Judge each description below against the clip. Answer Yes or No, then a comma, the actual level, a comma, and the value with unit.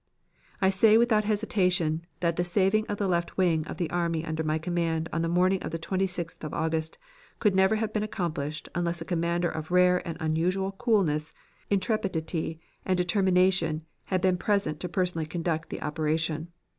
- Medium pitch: Yes, medium, 175 Hz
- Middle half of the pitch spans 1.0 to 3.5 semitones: Yes, average, 2.9 semitones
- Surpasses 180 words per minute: No, average, 175 wpm